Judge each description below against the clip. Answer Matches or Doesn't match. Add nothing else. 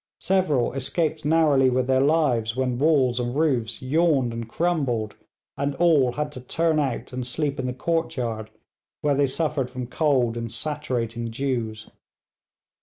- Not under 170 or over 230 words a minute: Doesn't match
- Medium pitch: Doesn't match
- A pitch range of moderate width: Matches